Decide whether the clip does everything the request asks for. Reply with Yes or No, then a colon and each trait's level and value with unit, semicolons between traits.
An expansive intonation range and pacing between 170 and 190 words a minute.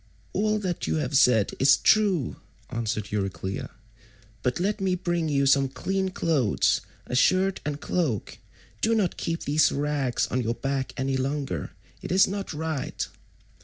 No: wide, 6.1 semitones; average, 150 wpm